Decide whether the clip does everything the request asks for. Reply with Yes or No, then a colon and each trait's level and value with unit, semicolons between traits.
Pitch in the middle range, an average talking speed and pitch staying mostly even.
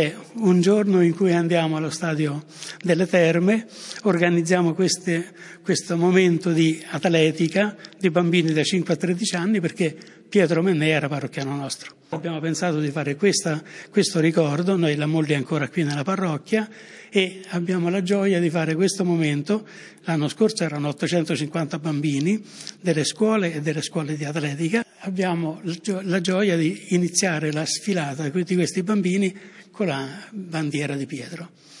No: medium, 170 Hz; average, 145 wpm; average, 3.1 semitones